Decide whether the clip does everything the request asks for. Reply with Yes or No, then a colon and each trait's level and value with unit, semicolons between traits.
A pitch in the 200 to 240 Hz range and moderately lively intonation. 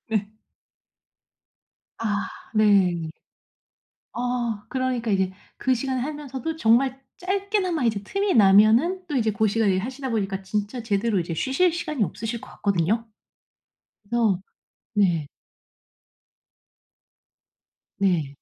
Yes: high, 225 Hz; average, 4.7 semitones